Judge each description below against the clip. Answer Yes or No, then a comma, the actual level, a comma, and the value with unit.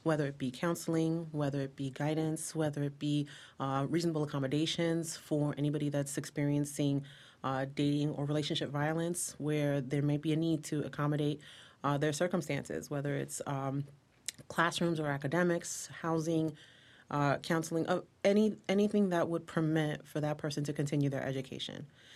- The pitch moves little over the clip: Yes, narrow, 2.3 semitones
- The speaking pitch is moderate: Yes, medium, 150 Hz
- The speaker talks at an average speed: Yes, average, 150 wpm